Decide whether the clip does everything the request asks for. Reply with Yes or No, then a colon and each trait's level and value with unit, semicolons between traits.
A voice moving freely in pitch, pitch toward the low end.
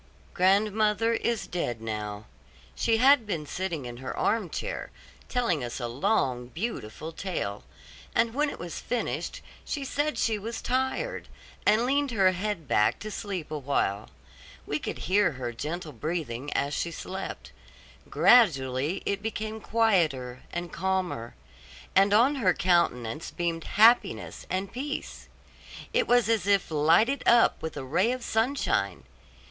No: wide, 7.7 semitones; medium, 185 Hz